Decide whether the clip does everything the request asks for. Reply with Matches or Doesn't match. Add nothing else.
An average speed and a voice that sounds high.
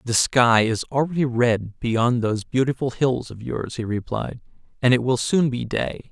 Doesn't match